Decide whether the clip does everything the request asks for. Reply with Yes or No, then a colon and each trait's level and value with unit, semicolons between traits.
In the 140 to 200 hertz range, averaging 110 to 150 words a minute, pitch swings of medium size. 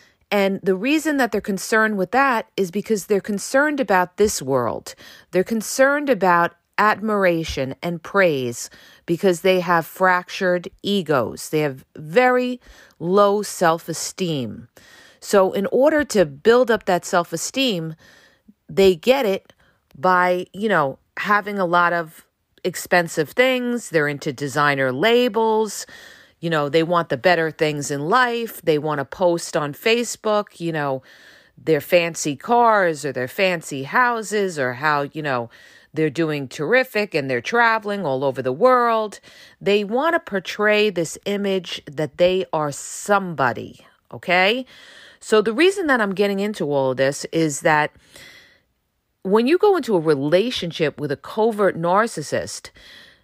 No: medium, 185 Hz; average, 145 wpm; wide, 5.7 semitones